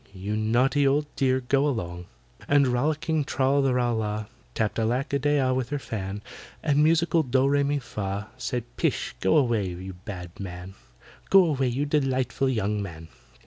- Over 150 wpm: Yes, average, 175 wpm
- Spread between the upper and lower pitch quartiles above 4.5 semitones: Yes, average, 5.3 semitones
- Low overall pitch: Yes, low, 125 Hz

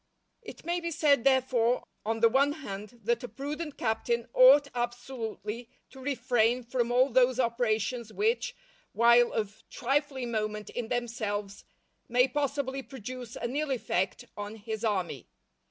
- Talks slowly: No, average, 145 wpm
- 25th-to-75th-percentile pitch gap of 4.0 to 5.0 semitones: No, average, 3.1 semitones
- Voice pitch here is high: Yes, high, 245 Hz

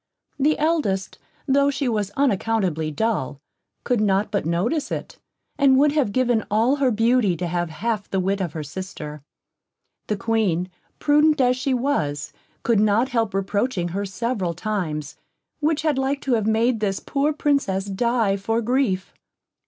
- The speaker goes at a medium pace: Yes, average, 160 wpm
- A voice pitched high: Yes, high, 220 Hz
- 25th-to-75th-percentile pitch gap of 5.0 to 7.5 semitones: Yes, wide, 5.6 semitones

